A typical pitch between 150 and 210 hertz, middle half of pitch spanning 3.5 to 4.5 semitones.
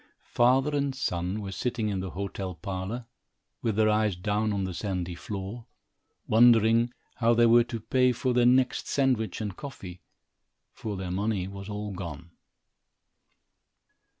No: low, 105 Hz; average, 4.0 semitones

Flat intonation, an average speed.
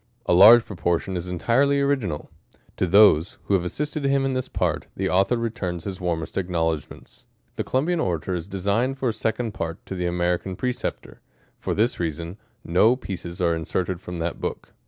No: wide, 5.4 semitones; average, 180 wpm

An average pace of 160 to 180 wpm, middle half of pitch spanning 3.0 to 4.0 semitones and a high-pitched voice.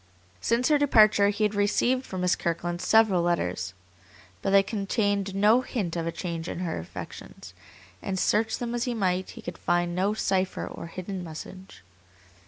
Yes: average, 175 wpm; average, 3.7 semitones; high, 195 Hz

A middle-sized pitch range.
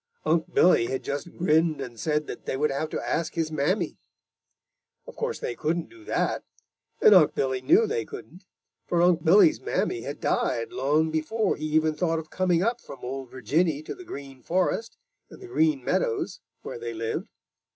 No: wide, 7.3 semitones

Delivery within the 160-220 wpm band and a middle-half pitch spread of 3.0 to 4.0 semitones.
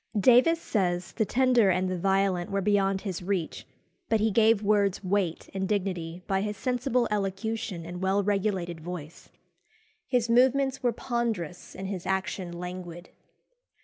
No: average, 145 wpm; average, 3.6 semitones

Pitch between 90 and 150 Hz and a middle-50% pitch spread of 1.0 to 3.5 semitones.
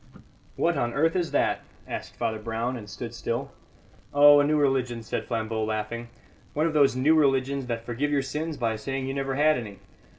No: low, 135 Hz; average, 4.0 semitones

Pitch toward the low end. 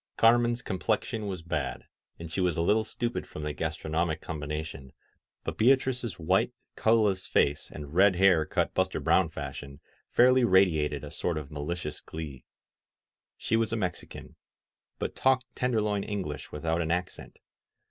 Yes: very low, 90 Hz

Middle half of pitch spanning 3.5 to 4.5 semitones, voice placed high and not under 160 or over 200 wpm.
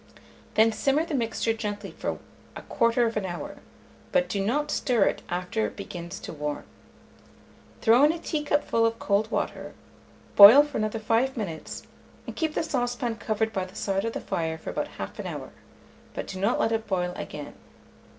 Yes: average, 3.9 semitones; high, 225 Hz; average, 170 wpm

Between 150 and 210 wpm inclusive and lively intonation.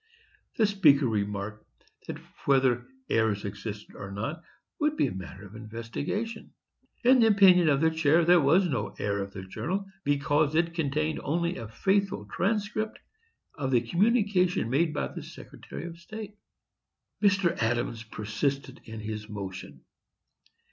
No: average, 140 wpm; wide, 8.7 semitones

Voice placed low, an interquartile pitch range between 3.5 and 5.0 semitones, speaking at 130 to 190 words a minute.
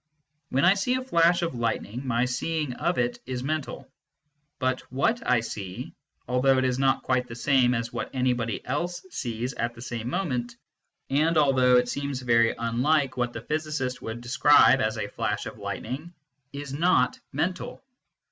Yes: low, 130 Hz; average, 3.9 semitones; average, 170 wpm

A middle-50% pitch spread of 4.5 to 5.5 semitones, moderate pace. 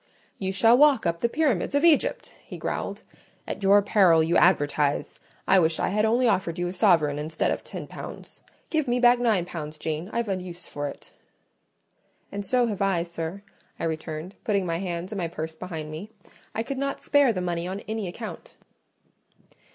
Yes: average, 5.1 semitones; average, 190 wpm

